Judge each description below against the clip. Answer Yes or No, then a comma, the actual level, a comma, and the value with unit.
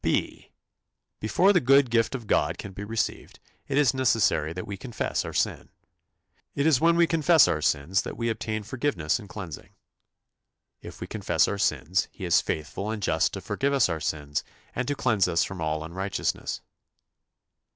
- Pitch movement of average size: No, wide, 7.2 semitones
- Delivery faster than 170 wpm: Yes, average, 180 wpm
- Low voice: Yes, low, 105 Hz